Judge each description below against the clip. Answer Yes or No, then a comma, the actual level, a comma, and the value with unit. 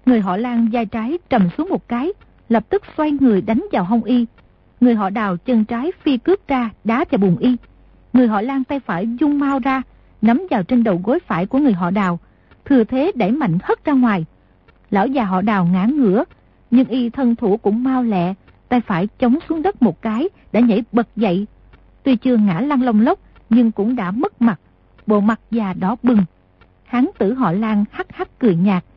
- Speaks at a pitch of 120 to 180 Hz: No, high, 235 Hz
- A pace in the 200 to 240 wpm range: Yes, average, 210 wpm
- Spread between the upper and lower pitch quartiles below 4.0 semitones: No, average, 4.3 semitones